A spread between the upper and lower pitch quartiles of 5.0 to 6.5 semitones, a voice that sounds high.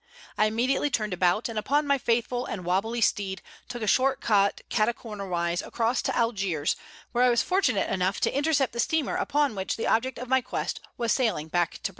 No: average, 4.5 semitones; high, 230 Hz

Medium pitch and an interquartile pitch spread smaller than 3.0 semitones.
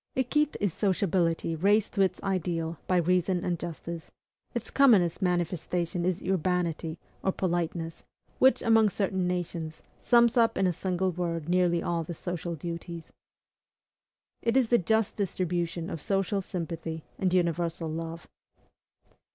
Yes: medium, 175 Hz; narrow, 2.4 semitones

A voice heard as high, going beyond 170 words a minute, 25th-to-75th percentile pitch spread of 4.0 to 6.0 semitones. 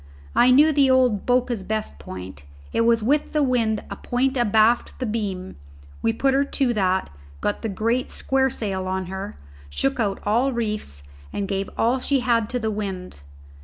Yes: high, 225 Hz; average, 180 wpm; average, 4.4 semitones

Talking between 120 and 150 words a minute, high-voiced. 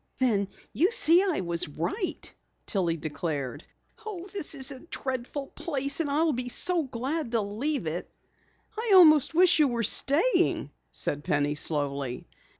Yes: average, 145 wpm; very high, 260 Hz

